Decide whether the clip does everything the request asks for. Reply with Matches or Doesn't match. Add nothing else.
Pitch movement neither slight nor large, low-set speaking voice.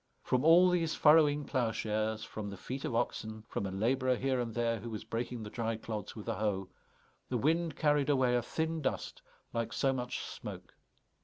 Matches